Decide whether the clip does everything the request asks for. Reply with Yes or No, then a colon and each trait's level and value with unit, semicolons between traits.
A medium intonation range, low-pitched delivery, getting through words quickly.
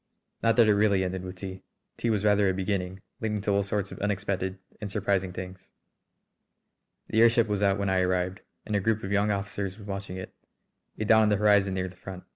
No: narrow, 1.9 semitones; low, 100 Hz; fast, 220 wpm